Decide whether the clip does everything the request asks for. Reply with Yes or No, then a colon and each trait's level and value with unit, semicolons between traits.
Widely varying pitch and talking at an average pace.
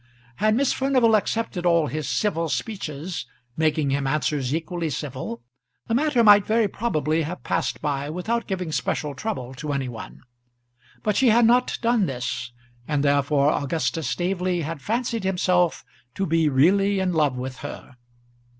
Yes: wide, 6.5 semitones; average, 155 wpm